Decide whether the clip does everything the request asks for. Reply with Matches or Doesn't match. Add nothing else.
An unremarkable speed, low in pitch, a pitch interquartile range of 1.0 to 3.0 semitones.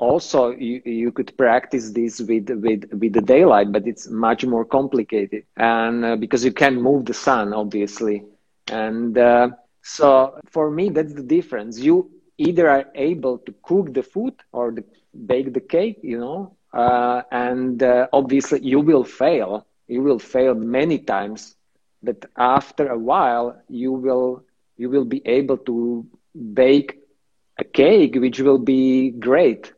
Matches